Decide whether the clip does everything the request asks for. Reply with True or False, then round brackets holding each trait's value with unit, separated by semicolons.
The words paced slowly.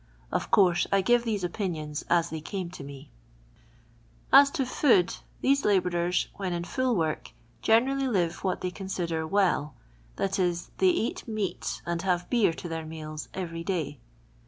False (160 wpm)